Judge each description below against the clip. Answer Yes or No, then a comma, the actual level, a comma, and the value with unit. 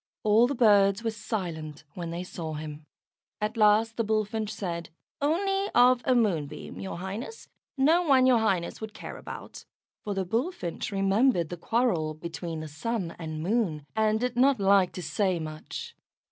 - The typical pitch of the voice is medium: No, high, 205 Hz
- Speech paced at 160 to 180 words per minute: Yes, average, 165 wpm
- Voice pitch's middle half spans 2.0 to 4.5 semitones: No, wide, 5.5 semitones